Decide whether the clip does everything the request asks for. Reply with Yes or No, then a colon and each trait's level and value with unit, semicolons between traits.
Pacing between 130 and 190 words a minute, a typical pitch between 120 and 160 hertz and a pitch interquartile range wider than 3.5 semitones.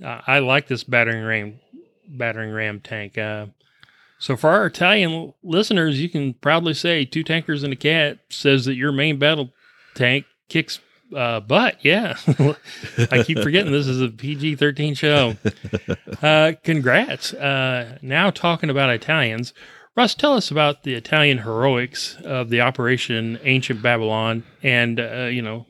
Yes: average, 150 wpm; low, 135 Hz; average, 4.5 semitones